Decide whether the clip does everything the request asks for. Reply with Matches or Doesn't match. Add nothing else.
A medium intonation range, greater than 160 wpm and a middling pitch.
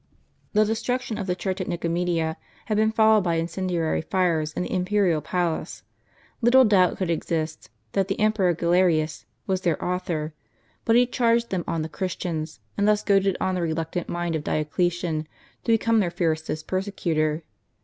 Matches